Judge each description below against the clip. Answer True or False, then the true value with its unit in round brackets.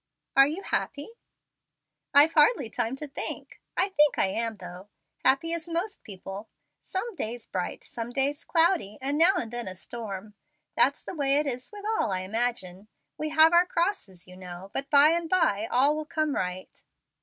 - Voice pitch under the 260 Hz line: False (275 Hz)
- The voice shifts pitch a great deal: True (7.5 semitones)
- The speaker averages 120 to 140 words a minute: False (185 wpm)